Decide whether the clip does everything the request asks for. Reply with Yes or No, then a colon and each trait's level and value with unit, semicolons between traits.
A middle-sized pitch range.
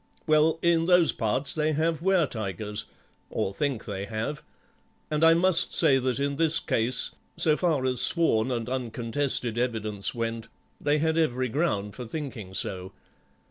No: wide, 5.9 semitones